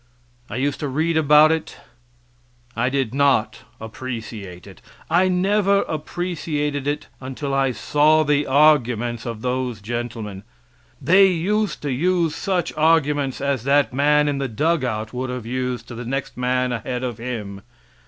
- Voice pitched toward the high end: No, low, 135 Hz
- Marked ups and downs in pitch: No, average, 4.0 semitones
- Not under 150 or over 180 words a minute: Yes, average, 155 wpm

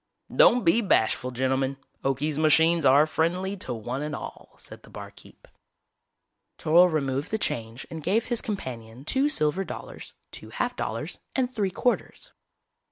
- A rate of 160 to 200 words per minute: No, average, 150 wpm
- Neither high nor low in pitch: Yes, medium, 155 Hz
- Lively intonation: Yes, wide, 6.6 semitones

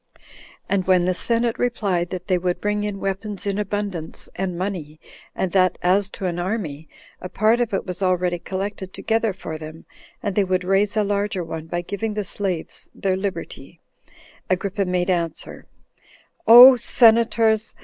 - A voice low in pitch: No, high, 190 Hz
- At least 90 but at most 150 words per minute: No, average, 160 wpm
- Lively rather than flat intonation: No, narrow, 2.6 semitones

